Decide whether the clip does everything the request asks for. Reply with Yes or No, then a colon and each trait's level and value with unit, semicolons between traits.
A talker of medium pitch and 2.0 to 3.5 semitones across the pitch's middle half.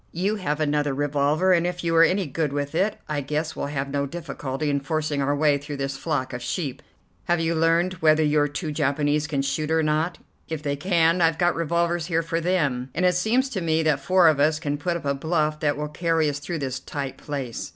Yes: medium, 155 Hz; average, 2.7 semitones